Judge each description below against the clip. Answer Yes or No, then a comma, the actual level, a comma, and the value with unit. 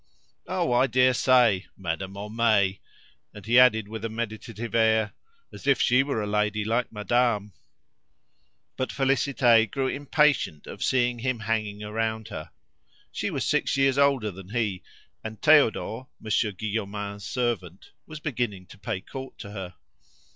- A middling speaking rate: Yes, average, 145 wpm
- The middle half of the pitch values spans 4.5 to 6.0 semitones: No, average, 3.5 semitones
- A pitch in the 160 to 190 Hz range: No, low, 110 Hz